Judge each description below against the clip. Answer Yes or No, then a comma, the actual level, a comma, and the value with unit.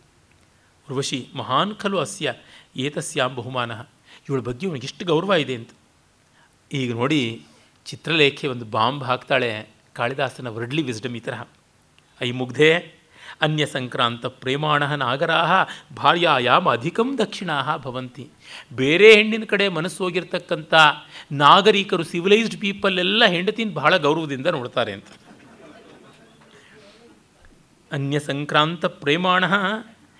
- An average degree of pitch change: No, wide, 6.1 semitones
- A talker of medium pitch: Yes, medium, 150 Hz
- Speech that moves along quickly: No, average, 85 wpm